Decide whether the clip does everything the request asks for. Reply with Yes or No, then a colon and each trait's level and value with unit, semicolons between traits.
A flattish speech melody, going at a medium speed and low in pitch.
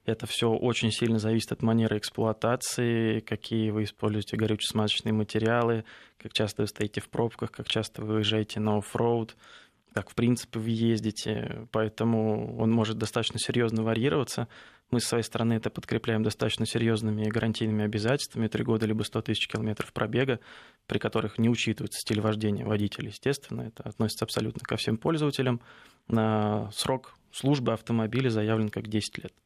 Yes: narrow, 1.4 semitones; average, 150 wpm; low, 110 Hz